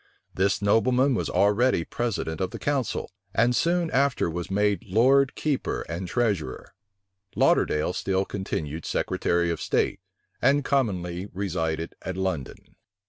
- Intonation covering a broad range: Yes, wide, 6.3 semitones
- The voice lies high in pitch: No, low, 100 Hz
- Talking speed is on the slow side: Yes, slow, 130 wpm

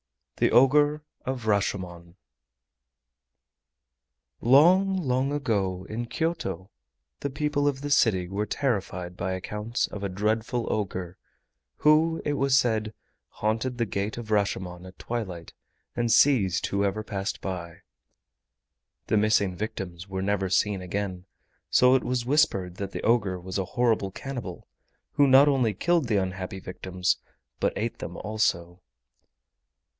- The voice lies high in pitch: No, low, 105 Hz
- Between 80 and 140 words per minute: Yes, slow, 135 wpm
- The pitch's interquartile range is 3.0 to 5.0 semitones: No, wide, 5.6 semitones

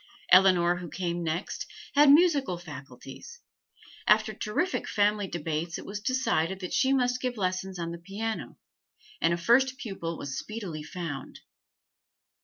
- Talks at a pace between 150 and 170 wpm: No, average, 140 wpm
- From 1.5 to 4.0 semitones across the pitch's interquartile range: No, average, 5.2 semitones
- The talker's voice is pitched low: No, high, 190 Hz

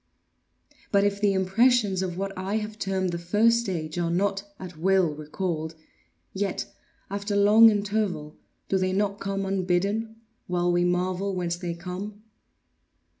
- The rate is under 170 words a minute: Yes, average, 145 wpm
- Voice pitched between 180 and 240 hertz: Yes, high, 190 Hz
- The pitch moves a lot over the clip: No, narrow, 2.4 semitones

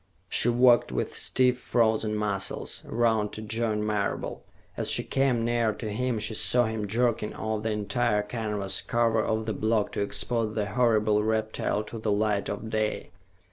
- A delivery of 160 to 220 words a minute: Yes, average, 170 wpm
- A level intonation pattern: Yes, narrow, 1.8 semitones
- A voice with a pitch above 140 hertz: No, low, 110 Hz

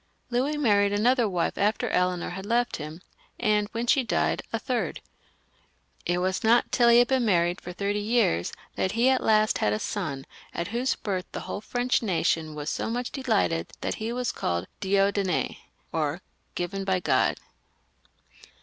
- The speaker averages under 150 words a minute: No, average, 170 wpm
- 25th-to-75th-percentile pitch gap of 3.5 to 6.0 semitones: Yes, average, 5.1 semitones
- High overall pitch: Yes, high, 200 Hz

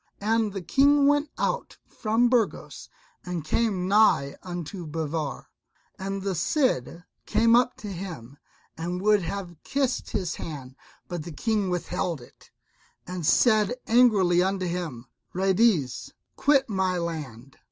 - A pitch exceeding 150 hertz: Yes, medium, 185 Hz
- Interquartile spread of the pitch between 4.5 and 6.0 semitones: Yes, average, 5.0 semitones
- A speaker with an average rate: No, slow, 130 wpm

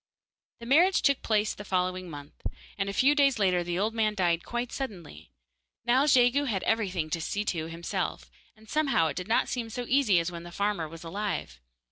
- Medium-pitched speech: No, high, 200 Hz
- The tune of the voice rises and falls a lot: Yes, wide, 5.8 semitones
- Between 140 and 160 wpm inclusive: No, average, 200 wpm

